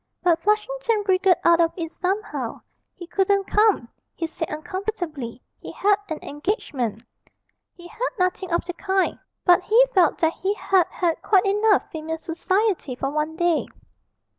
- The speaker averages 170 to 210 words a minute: No, average, 155 wpm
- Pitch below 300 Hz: No, very high, 365 Hz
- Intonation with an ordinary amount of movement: Yes, average, 3.8 semitones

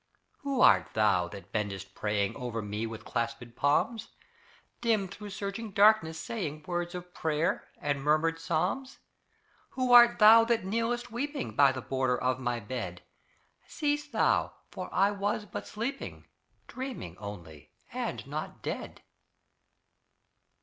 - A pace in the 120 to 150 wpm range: Yes, slow, 135 wpm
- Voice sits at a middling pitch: Yes, medium, 165 Hz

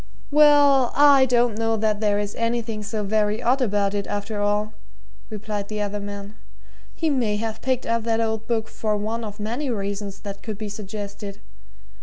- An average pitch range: No, narrow, 2.1 semitones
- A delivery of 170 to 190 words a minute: Yes, average, 180 wpm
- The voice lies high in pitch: Yes, high, 215 Hz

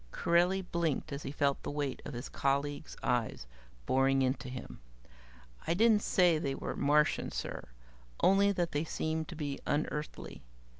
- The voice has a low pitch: No, medium, 150 Hz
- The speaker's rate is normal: Yes, average, 155 wpm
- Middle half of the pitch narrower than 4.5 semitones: Yes, average, 3.7 semitones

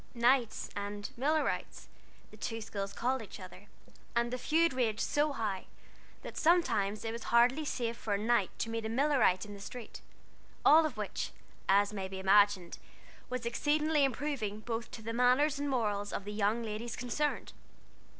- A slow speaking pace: No, average, 170 wpm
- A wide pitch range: No, average, 4.1 semitones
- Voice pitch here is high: Yes, high, 230 Hz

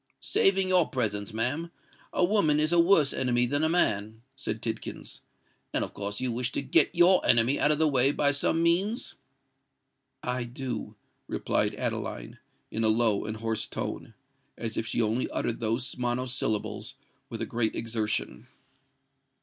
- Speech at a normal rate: Yes, average, 160 wpm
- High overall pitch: No, low, 125 Hz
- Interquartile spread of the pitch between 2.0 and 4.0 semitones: No, average, 5.3 semitones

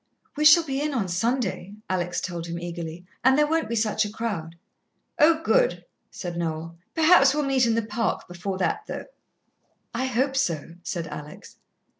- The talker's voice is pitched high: Yes, high, 215 Hz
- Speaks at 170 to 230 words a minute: Yes, average, 175 wpm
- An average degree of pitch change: No, wide, 7.7 semitones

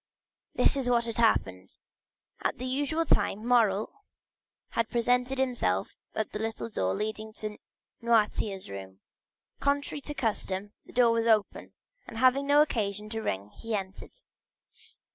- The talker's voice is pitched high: Yes, high, 225 Hz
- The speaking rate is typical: Yes, average, 145 wpm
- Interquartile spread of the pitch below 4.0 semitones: Yes, average, 3.6 semitones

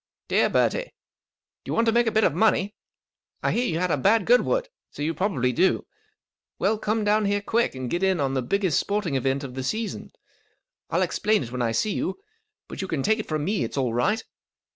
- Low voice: No, high, 195 Hz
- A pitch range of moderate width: No, wide, 7.8 semitones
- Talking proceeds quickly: Yes, fast, 220 wpm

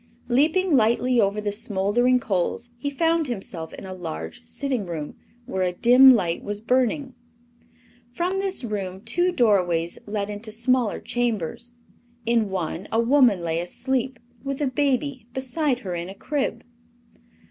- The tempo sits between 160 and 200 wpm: No, average, 145 wpm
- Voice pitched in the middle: No, high, 235 Hz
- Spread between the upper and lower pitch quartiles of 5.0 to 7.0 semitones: Yes, wide, 5.5 semitones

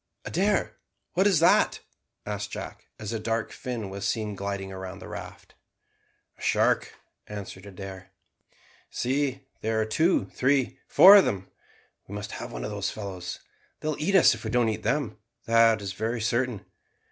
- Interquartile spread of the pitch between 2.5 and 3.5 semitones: No, average, 5.0 semitones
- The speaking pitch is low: Yes, low, 110 Hz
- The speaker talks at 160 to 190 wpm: Yes, average, 170 wpm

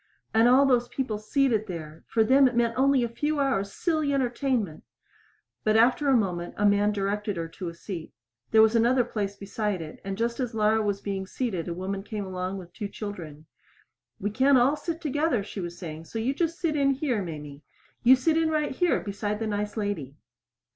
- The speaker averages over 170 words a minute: Yes, fast, 205 wpm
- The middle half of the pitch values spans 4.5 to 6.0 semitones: Yes, average, 5.0 semitones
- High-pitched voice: Yes, high, 215 Hz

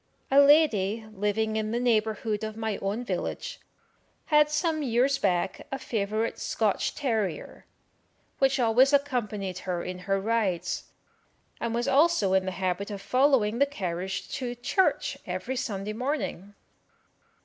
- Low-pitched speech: No, high, 220 Hz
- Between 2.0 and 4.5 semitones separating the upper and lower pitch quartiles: No, average, 5.0 semitones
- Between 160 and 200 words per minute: No, average, 140 wpm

